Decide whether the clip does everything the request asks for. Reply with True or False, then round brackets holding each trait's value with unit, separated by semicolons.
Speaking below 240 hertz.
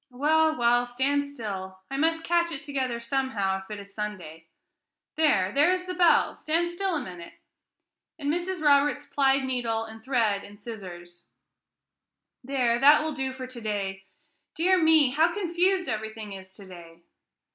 False (260 Hz)